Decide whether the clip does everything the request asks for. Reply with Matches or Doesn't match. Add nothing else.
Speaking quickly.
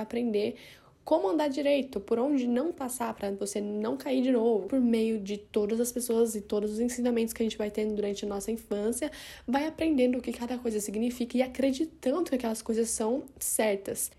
Matches